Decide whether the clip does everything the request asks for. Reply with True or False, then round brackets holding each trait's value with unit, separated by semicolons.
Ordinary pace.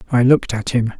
False (240 wpm)